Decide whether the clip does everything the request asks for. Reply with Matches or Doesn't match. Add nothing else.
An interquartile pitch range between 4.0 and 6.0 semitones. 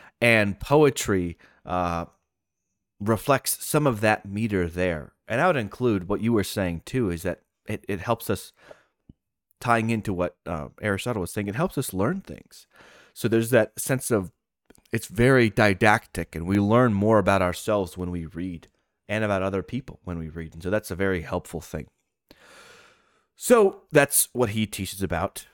Matches